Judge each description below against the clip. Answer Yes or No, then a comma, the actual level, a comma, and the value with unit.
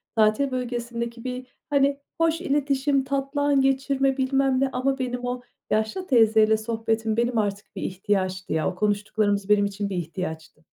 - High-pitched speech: Yes, high, 235 Hz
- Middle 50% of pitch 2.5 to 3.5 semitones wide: No, average, 4.4 semitones